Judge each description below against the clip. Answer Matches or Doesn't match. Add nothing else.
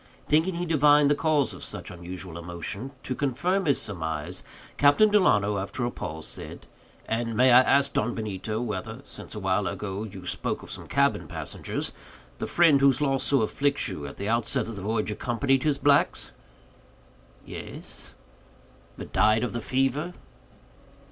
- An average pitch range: Doesn't match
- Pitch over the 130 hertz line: Doesn't match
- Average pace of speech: Matches